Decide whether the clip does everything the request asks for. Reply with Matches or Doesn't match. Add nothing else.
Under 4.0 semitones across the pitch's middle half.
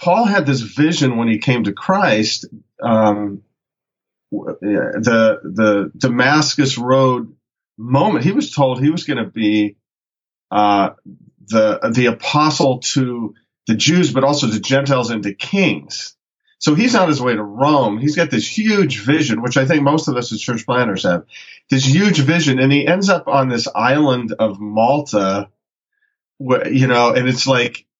Doesn't match